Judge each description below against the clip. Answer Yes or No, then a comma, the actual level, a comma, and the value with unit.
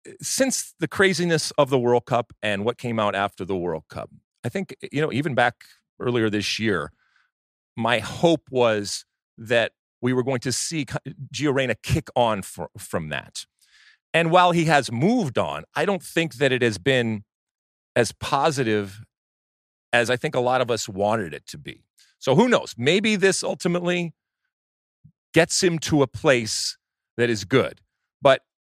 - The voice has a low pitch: Yes, low, 130 Hz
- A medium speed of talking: Yes, average, 165 wpm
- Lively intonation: Yes, wide, 6.7 semitones